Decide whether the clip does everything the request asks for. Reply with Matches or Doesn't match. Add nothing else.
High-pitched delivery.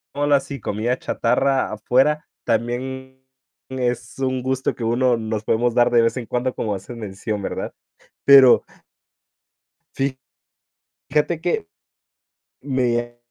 Doesn't match